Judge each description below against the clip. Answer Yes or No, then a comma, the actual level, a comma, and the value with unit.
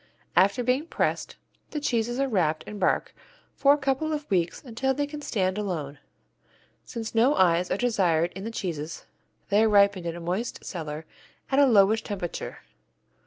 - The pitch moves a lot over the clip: Yes, wide, 6.2 semitones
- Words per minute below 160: No, average, 170 wpm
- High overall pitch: Yes, high, 205 Hz